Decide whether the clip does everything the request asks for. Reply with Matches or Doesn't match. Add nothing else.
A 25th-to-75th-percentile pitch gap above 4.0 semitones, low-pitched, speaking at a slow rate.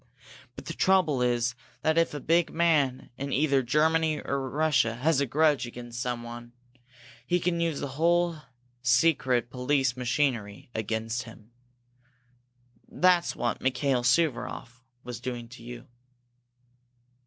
Matches